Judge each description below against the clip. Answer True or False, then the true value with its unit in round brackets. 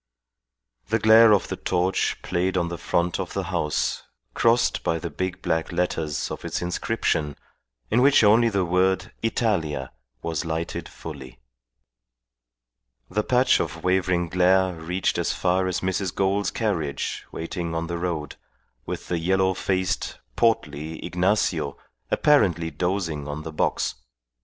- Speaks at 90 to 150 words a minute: True (140 wpm)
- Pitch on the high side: False (90 Hz)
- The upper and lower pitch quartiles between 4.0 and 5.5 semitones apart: False (2.8 semitones)